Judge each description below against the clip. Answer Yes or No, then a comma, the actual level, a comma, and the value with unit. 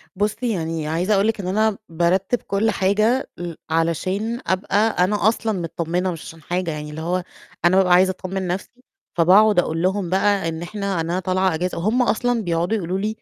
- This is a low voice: No, medium, 185 Hz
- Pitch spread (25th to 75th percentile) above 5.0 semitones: No, average, 3.5 semitones